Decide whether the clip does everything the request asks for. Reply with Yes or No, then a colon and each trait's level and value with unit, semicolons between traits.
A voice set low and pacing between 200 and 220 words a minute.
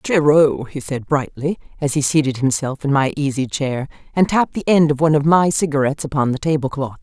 No: medium, 145 Hz; fast, 205 wpm